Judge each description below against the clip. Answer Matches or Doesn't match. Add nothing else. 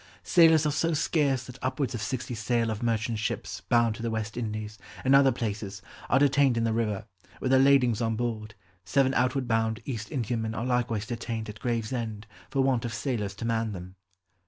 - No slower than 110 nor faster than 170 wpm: Doesn't match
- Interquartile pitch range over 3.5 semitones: Doesn't match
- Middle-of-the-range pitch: Doesn't match